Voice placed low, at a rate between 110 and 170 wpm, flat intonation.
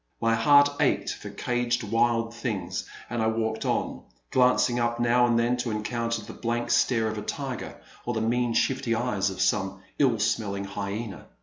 No: low, 115 Hz; average, 180 wpm; narrow, 2.1 semitones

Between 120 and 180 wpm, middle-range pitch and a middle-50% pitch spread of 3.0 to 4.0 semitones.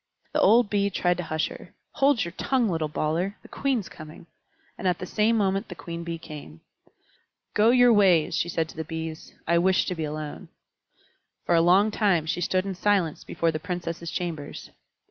No: average, 195 wpm; medium, 175 Hz; average, 3.7 semitones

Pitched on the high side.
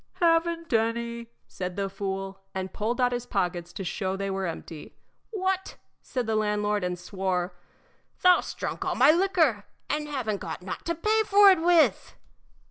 Yes: high, 225 Hz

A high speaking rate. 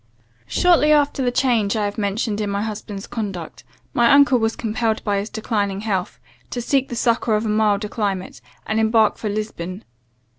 No: average, 180 wpm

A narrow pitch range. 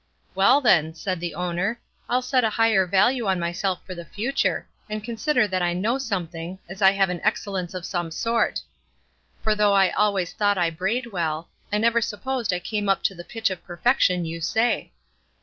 No: average, 4.2 semitones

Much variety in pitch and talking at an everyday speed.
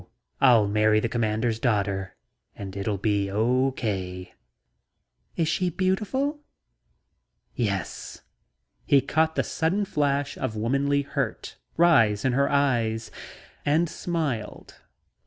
No: wide, 6.1 semitones; slow, 110 wpm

